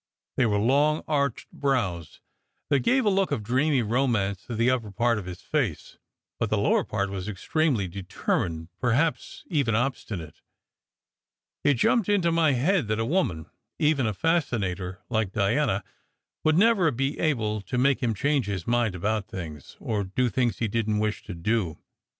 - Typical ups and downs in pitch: No, wide, 6.0 semitones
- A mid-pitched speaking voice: No, low, 115 Hz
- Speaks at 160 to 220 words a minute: Yes, average, 170 wpm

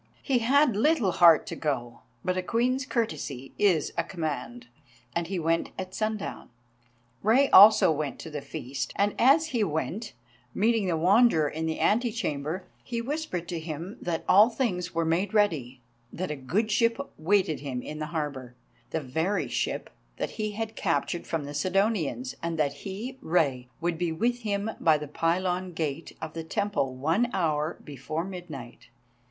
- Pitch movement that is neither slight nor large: No, wide, 5.7 semitones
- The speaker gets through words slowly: No, average, 170 wpm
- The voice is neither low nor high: Yes, medium, 175 Hz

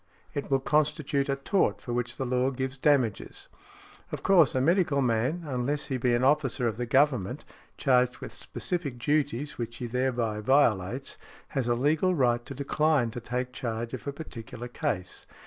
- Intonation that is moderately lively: Yes, average, 3.2 semitones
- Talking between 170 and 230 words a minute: Yes, average, 175 wpm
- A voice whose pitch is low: Yes, low, 130 Hz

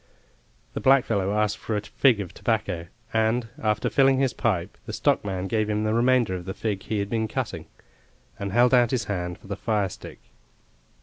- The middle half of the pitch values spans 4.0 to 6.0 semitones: No, average, 2.9 semitones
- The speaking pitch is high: No, low, 105 Hz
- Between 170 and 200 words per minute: Yes, average, 185 wpm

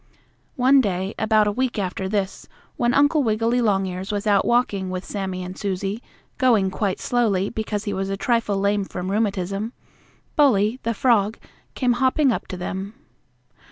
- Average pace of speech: Yes, average, 160 wpm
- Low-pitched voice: No, high, 205 Hz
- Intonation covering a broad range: No, average, 3.6 semitones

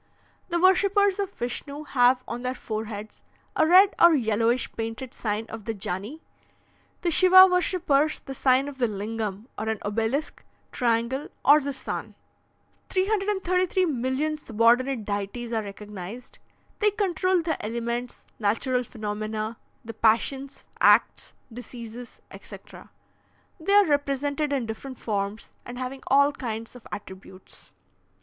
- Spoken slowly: Yes, slow, 130 wpm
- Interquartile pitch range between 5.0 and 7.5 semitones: Yes, wide, 5.6 semitones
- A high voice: Yes, very high, 250 Hz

